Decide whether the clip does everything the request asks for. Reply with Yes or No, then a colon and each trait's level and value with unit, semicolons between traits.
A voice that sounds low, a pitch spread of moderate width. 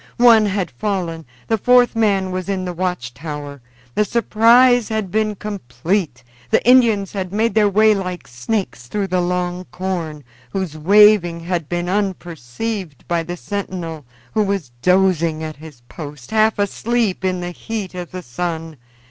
No: medium, 185 Hz; average, 4.3 semitones